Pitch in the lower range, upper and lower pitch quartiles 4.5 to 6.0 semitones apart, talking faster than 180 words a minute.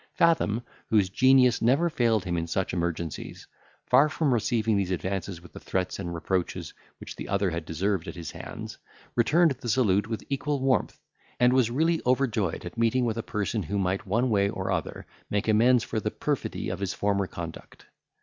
Yes: low, 105 Hz; average, 5.0 semitones; average, 190 wpm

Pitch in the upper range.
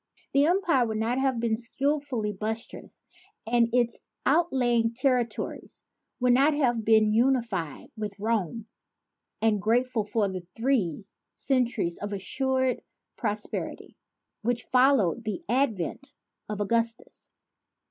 Yes: high, 235 Hz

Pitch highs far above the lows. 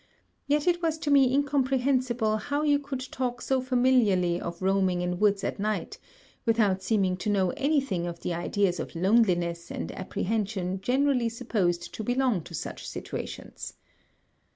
Yes: wide, 6.0 semitones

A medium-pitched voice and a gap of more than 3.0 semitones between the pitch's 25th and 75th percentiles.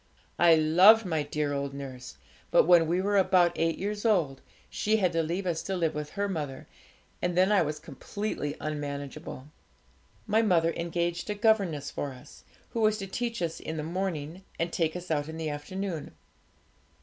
Yes: medium, 170 Hz; average, 4.2 semitones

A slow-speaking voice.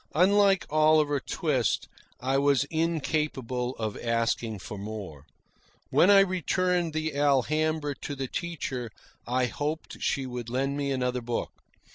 Yes: slow, 130 wpm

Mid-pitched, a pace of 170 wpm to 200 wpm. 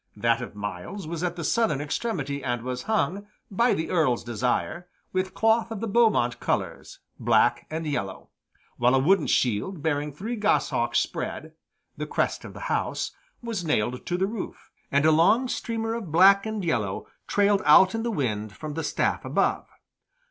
Yes: medium, 165 Hz; average, 175 wpm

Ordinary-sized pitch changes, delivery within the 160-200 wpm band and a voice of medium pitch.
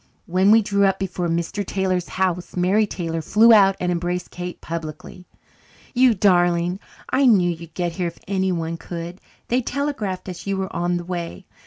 No: narrow, 2.3 semitones; average, 175 wpm; medium, 180 Hz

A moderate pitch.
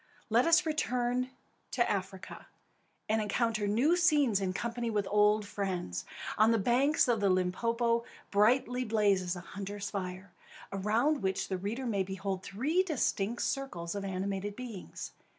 No: high, 210 Hz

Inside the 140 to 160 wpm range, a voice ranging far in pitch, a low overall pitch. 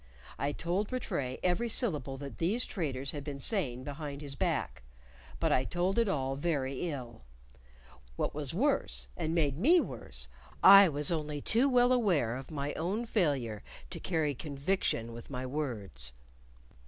No: average, 155 wpm; wide, 6.1 semitones; medium, 150 Hz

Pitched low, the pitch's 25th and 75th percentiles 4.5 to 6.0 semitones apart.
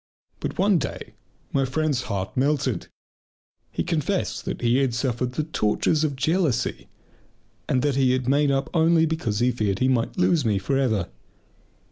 No: low, 130 Hz; average, 4.0 semitones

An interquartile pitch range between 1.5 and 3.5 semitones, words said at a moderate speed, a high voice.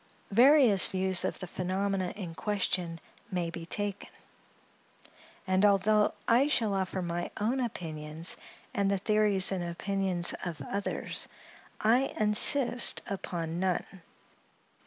No: average, 2.9 semitones; slow, 115 wpm; high, 195 Hz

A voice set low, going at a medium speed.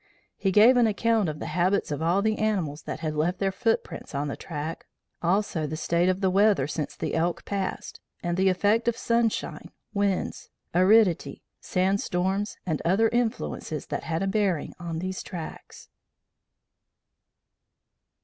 No: medium, 185 Hz; average, 160 wpm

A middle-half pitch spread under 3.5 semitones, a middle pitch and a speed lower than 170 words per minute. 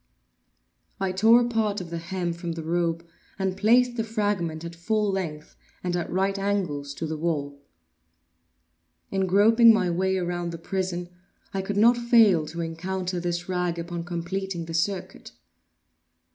Yes: average, 3.0 semitones; medium, 180 Hz; average, 160 wpm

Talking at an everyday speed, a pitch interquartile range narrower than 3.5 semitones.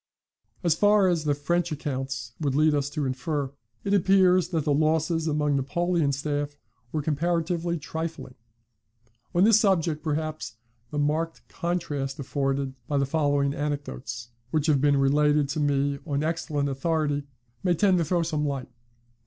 Yes: average, 155 wpm; average, 2.9 semitones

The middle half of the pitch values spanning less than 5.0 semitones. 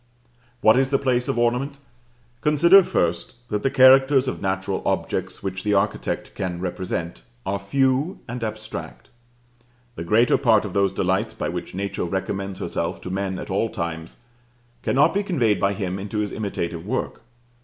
No: wide, 5.4 semitones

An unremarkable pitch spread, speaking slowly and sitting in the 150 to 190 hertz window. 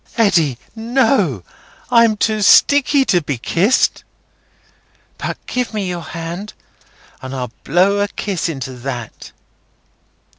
No: wide, 7.6 semitones; slow, 115 wpm; medium, 185 Hz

